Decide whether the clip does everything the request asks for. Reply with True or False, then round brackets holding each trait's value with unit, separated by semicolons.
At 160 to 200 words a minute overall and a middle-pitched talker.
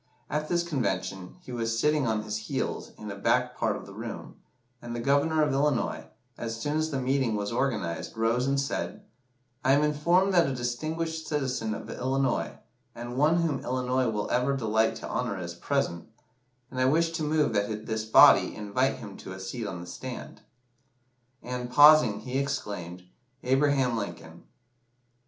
False (175 wpm; 125 Hz)